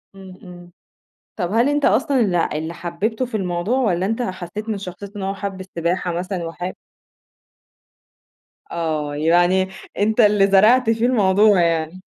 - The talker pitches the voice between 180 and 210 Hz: Yes, high, 190 Hz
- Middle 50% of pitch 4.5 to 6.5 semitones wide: No, average, 3.7 semitones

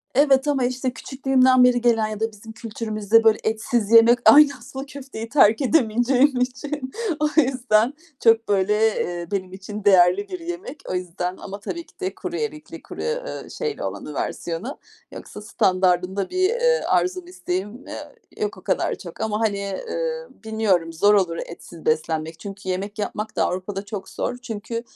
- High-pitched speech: Yes, high, 225 Hz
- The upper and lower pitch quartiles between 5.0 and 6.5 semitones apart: Yes, wide, 5.4 semitones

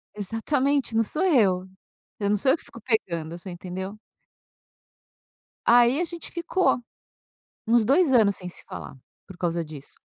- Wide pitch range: Yes, wide, 6.6 semitones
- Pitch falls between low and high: No, high, 220 Hz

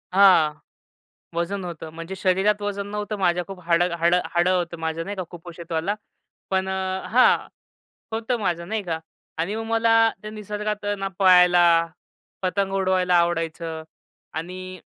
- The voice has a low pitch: No, medium, 185 Hz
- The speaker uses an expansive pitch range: No, average, 2.8 semitones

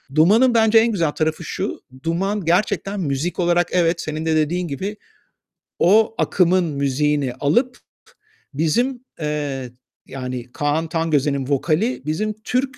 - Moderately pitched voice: Yes, medium, 165 Hz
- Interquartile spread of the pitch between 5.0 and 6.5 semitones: Yes, wide, 5.6 semitones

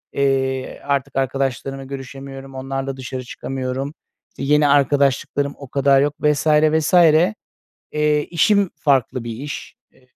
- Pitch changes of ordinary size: No, narrow, 1.5 semitones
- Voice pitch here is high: No, low, 135 Hz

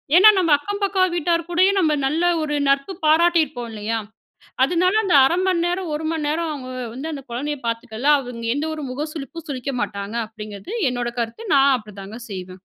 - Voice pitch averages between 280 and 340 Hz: Yes, very high, 295 Hz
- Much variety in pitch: Yes, wide, 6.3 semitones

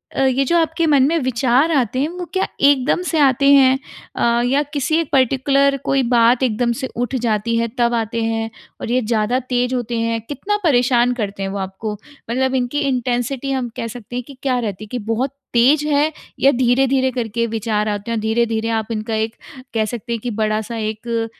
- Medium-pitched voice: No, high, 245 Hz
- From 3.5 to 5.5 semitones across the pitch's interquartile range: No, average, 3.0 semitones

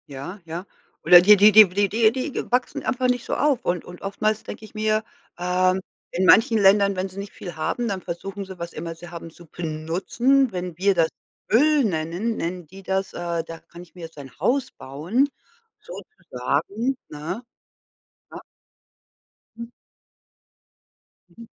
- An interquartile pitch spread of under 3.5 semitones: No, average, 4.5 semitones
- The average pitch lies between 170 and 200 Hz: Yes, high, 190 Hz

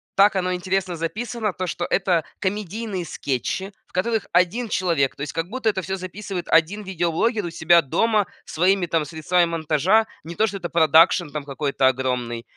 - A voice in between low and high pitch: Yes, medium, 180 Hz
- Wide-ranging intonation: No, average, 3.7 semitones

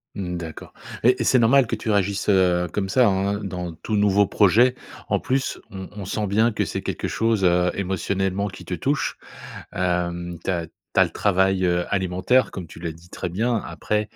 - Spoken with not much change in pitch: No, average, 3.1 semitones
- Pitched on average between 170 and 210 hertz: No, very low, 95 Hz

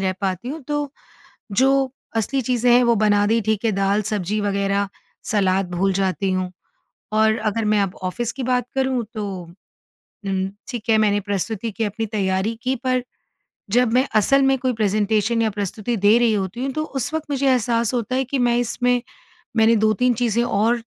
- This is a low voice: No, high, 225 Hz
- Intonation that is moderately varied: Yes, average, 3.6 semitones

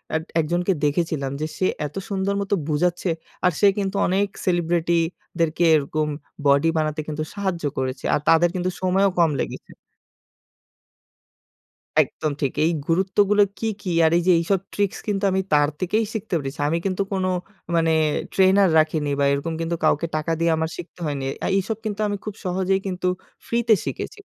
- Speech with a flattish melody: No, average, 3.6 semitones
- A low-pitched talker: No, medium, 175 Hz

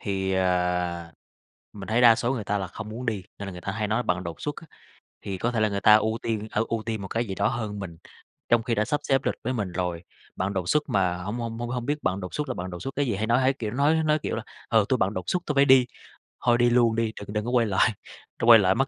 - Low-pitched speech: Yes, low, 110 Hz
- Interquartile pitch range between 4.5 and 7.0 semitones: No, average, 4.0 semitones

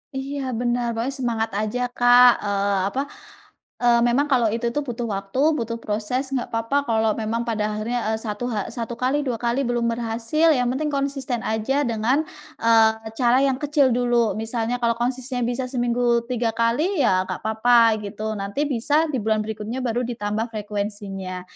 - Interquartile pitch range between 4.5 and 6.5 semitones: No, narrow, 2.5 semitones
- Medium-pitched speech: No, high, 235 Hz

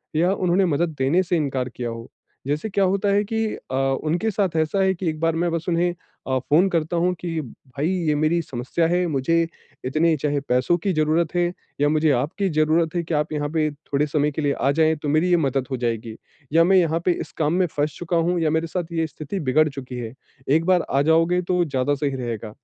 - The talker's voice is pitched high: No, medium, 155 Hz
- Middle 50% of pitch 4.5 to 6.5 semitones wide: No, average, 3.4 semitones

